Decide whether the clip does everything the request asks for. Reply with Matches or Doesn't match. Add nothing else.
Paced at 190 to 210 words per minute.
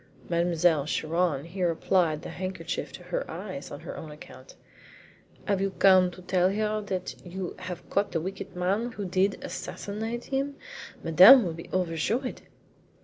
Doesn't match